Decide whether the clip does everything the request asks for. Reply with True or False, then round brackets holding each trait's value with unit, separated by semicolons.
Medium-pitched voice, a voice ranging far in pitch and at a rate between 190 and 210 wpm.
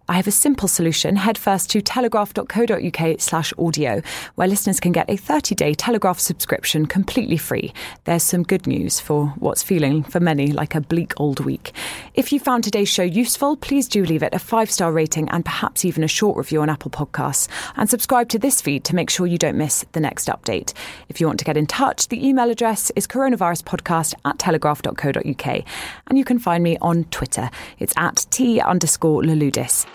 True (180 Hz; 6.0 semitones; 200 wpm)